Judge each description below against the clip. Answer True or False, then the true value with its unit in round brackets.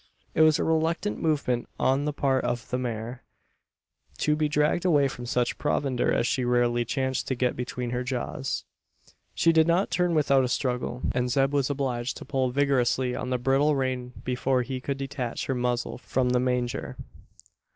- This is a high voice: False (130 Hz)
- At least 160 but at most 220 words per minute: True (180 wpm)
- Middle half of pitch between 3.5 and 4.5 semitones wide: False (2.5 semitones)